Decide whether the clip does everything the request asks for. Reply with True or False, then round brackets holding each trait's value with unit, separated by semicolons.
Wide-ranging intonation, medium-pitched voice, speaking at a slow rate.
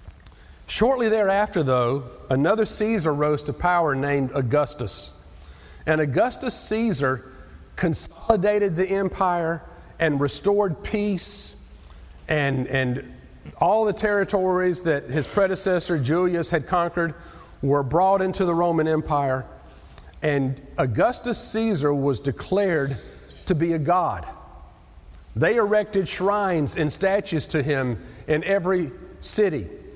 True (6.6 semitones; 165 Hz; 110 wpm)